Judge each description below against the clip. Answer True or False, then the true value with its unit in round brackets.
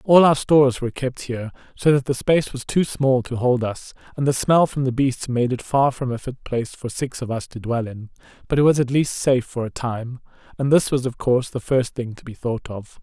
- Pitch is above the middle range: False (130 Hz)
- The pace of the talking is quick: True (265 wpm)